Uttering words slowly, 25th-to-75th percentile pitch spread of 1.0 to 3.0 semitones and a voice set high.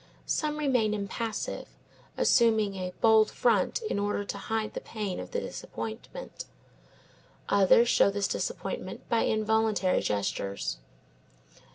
Yes: slow, 115 wpm; narrow, 2.6 semitones; high, 215 Hz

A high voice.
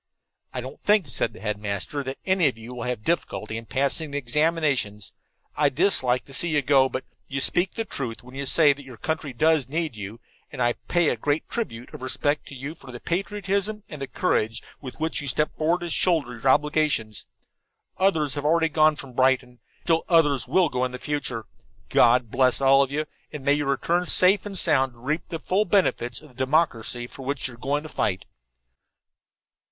No: medium, 140 Hz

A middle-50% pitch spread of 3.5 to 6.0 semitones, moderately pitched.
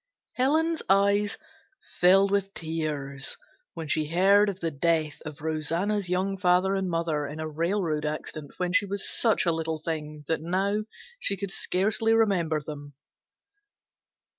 Yes: average, 4.2 semitones; medium, 175 Hz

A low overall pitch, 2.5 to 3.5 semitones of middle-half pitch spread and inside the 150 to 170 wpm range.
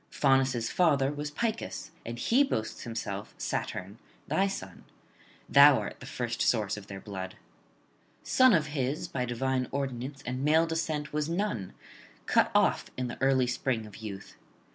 No: low, 130 Hz; average, 4.6 semitones; average, 155 wpm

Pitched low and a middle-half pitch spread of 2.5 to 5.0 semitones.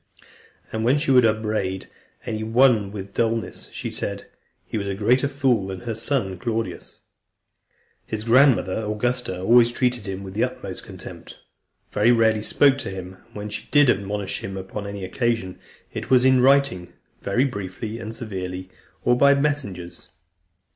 Yes: low, 110 Hz; average, 4.3 semitones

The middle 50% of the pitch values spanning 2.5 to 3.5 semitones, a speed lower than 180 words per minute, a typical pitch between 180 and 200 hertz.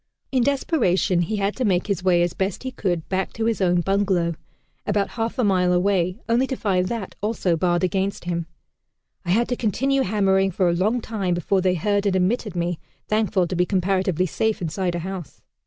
No: average, 3.1 semitones; fast, 205 wpm; high, 190 Hz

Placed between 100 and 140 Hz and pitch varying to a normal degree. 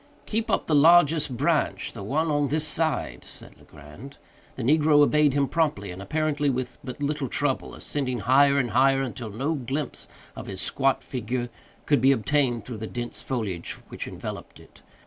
Yes: low, 135 Hz; average, 3.6 semitones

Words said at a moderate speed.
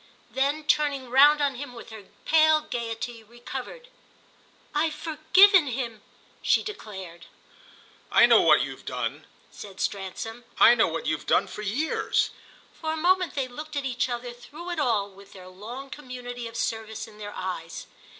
Yes: average, 160 wpm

